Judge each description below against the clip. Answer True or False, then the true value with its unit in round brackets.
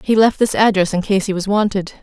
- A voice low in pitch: False (200 Hz)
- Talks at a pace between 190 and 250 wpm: False (265 wpm)